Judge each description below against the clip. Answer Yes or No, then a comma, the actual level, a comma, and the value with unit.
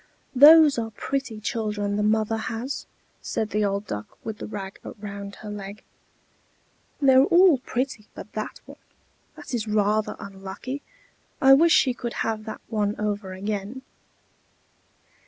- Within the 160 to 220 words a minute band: No, average, 140 wpm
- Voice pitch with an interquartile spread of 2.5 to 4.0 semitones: Yes, average, 3.7 semitones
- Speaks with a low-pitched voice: No, high, 215 Hz